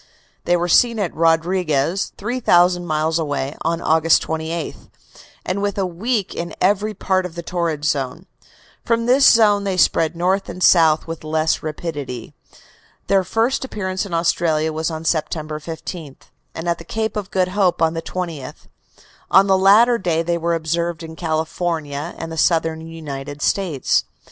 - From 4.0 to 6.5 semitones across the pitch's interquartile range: No, average, 3.0 semitones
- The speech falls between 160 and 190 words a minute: Yes, average, 165 wpm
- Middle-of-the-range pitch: Yes, medium, 170 Hz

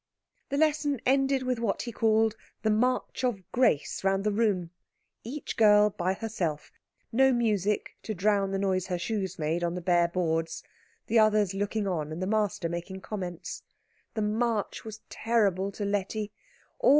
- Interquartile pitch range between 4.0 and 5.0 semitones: No, average, 3.4 semitones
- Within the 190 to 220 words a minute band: No, average, 160 wpm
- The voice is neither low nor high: No, high, 205 Hz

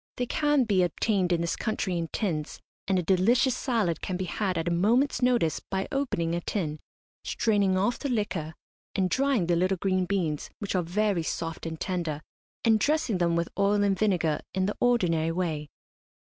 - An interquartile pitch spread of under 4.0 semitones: No, average, 4.3 semitones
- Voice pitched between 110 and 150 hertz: No, medium, 185 Hz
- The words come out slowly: No, average, 190 wpm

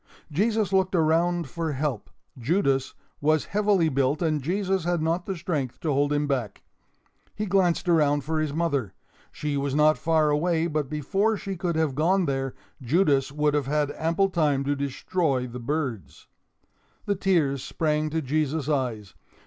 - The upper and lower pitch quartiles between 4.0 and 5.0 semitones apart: No, average, 3.6 semitones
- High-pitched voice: No, medium, 155 Hz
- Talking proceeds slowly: No, average, 165 wpm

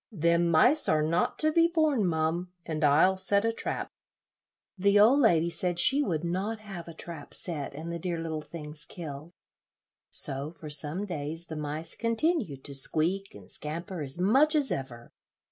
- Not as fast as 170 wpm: No, average, 175 wpm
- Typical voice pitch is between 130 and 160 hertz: No, medium, 170 Hz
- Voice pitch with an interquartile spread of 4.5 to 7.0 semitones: Yes, average, 4.8 semitones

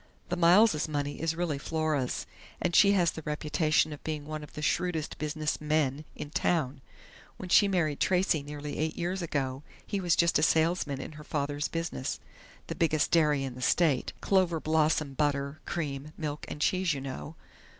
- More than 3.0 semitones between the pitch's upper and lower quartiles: No, narrow, 2.6 semitones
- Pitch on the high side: No, medium, 155 Hz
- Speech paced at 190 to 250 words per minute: No, average, 175 wpm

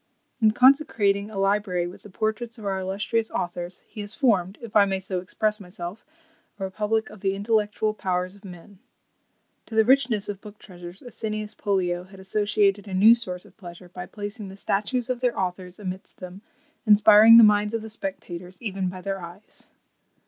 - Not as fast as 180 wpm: No, average, 185 wpm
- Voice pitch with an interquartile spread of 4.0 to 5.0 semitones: No, narrow, 2.5 semitones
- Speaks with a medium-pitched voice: No, high, 200 Hz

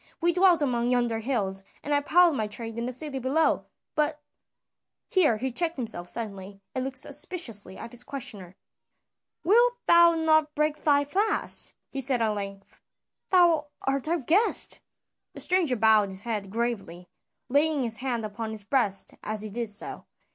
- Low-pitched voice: No, very high, 255 Hz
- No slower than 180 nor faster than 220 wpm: No, average, 170 wpm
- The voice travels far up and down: Yes, wide, 6.1 semitones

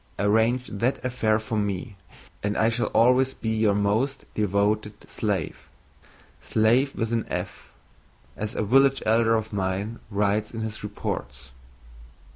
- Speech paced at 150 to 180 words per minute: No, slow, 135 wpm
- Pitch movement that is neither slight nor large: No, narrow, 2.2 semitones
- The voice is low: Yes, low, 110 Hz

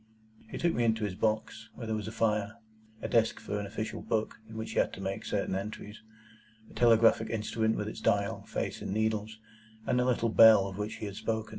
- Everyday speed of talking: No, fast, 225 wpm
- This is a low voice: Yes, low, 110 Hz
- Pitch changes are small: Yes, narrow, 1.3 semitones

